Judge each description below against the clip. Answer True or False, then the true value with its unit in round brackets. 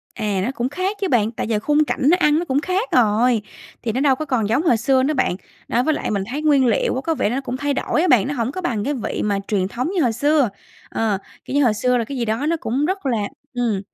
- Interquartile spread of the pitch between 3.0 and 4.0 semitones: False (4.7 semitones)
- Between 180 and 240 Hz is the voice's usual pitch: False (255 Hz)